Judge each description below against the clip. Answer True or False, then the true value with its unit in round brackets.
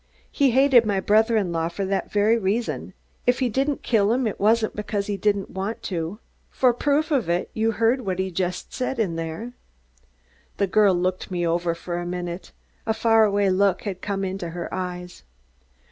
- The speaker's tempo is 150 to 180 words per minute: False (190 wpm)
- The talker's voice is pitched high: True (200 Hz)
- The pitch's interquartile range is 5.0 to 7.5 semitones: False (3.9 semitones)